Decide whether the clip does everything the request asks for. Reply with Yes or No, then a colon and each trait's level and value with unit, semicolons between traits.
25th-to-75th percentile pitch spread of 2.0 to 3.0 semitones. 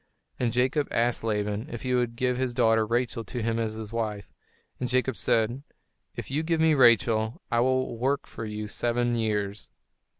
Yes: narrow, 2.4 semitones